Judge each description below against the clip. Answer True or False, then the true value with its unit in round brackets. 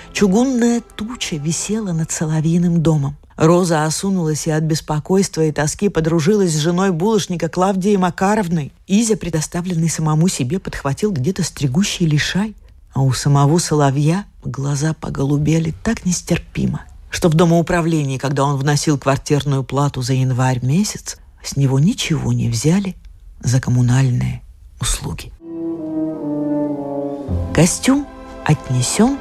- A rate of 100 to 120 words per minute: True (115 wpm)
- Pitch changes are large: False (4.4 semitones)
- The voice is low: False (160 Hz)